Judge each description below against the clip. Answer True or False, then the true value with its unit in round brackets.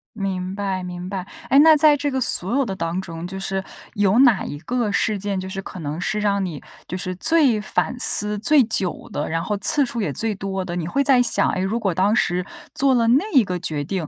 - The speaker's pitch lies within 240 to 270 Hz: False (195 Hz)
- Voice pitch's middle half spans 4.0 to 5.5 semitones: True (4.6 semitones)